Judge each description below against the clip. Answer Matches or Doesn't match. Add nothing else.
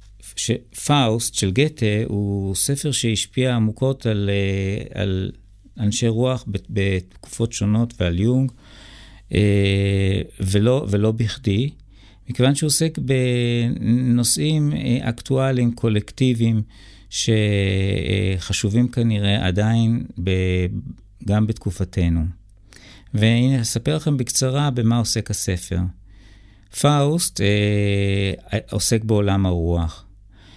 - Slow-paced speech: Matches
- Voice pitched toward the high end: Doesn't match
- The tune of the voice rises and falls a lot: Doesn't match